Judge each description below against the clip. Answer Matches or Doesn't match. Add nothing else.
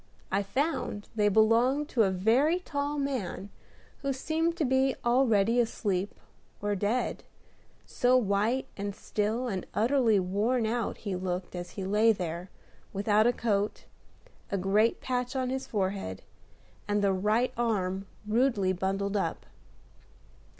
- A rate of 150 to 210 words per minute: Doesn't match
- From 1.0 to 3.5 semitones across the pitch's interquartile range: Doesn't match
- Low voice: Doesn't match